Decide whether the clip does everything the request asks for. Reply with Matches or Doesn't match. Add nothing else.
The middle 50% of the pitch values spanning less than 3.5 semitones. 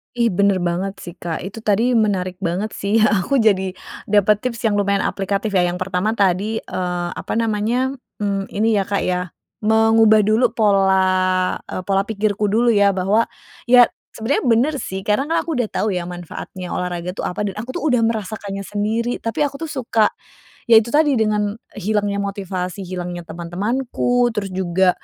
Matches